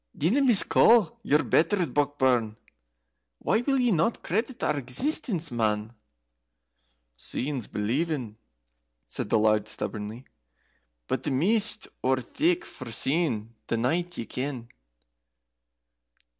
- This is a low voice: No, medium, 145 Hz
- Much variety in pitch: Yes, wide, 8.5 semitones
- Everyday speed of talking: No, slow, 110 wpm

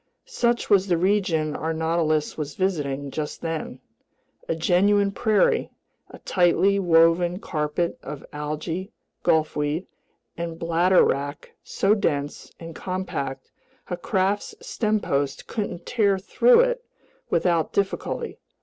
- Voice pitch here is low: No, medium, 170 Hz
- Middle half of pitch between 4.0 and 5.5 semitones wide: Yes, average, 4.3 semitones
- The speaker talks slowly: Yes, slow, 115 wpm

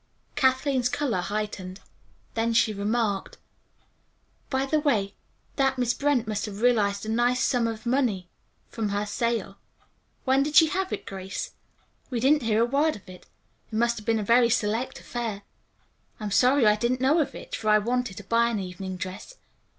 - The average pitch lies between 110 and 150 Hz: No, high, 230 Hz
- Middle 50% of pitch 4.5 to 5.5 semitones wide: No, average, 3.9 semitones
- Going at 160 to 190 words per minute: Yes, average, 180 wpm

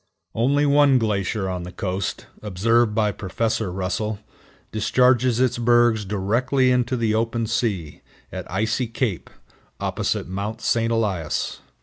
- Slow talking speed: Yes, slow, 125 wpm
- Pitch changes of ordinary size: Yes, average, 3.3 semitones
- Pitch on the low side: Yes, low, 110 Hz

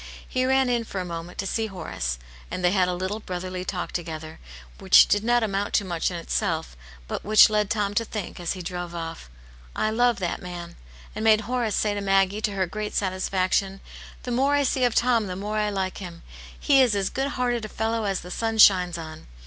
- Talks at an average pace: No, fast, 235 wpm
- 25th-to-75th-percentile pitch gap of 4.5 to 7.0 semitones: No, average, 3.7 semitones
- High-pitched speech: Yes, high, 200 Hz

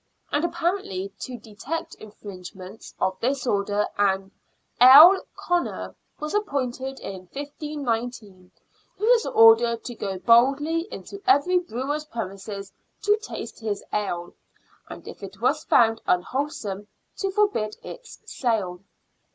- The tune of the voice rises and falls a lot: Yes, wide, 7.0 semitones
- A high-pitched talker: Yes, high, 240 Hz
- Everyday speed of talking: No, slow, 125 wpm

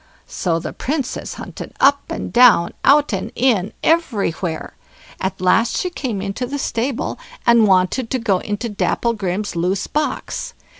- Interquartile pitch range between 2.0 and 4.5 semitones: No, wide, 5.6 semitones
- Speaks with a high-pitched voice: Yes, high, 225 Hz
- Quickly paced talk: No, average, 145 wpm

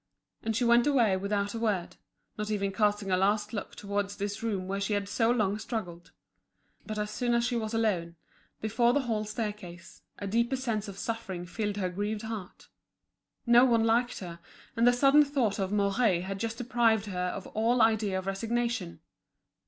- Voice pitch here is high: Yes, high, 215 Hz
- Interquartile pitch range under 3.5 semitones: Yes, average, 2.8 semitones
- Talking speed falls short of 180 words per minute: No, average, 185 wpm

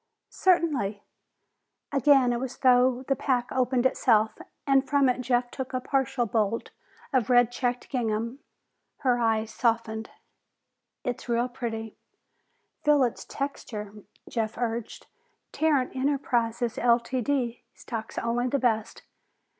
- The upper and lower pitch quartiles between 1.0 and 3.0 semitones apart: Yes, narrow, 2.4 semitones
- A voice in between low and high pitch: No, high, 245 Hz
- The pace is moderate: No, slow, 125 wpm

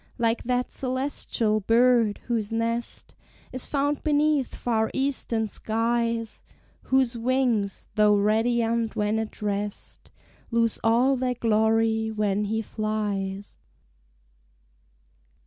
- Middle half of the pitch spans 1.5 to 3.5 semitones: Yes, narrow, 2.5 semitones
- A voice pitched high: Yes, high, 230 Hz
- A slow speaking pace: Yes, slow, 100 wpm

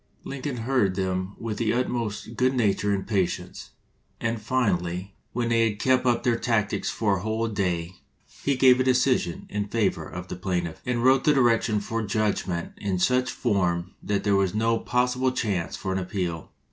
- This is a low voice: Yes, low, 110 Hz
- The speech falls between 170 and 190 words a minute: Yes, average, 180 wpm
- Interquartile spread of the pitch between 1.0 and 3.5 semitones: No, average, 4.4 semitones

